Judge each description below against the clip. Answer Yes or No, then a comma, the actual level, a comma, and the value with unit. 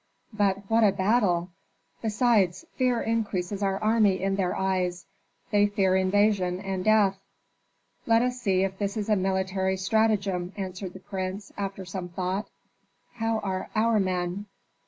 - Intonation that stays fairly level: Yes, narrow, 2.3 semitones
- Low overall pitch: No, high, 195 Hz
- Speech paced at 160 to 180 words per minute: No, average, 145 wpm